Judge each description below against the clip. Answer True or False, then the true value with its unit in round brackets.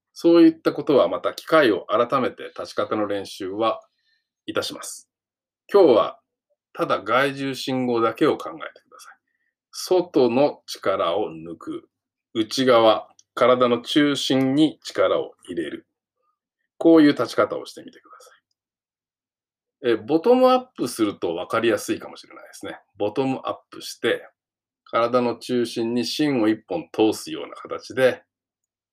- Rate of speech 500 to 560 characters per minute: False (270 characters per minute)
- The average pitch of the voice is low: False (145 Hz)